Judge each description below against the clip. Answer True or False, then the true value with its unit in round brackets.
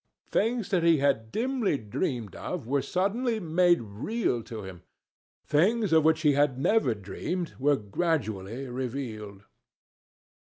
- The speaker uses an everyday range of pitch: False (8.2 semitones)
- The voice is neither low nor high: True (145 Hz)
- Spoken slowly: True (130 wpm)